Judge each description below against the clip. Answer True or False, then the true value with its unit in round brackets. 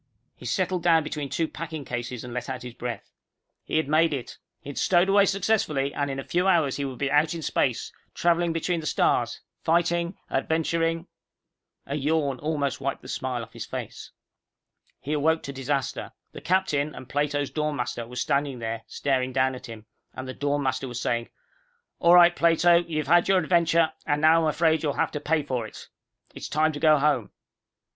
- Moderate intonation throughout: True (3.8 semitones)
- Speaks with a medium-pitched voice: True (150 Hz)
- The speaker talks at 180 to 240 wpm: True (195 wpm)